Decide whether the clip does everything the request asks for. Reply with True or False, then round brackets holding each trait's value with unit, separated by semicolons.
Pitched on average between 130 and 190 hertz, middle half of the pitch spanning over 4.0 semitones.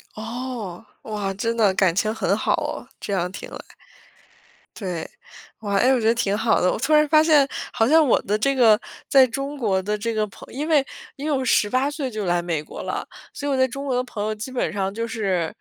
False (225 Hz; 4.7 semitones)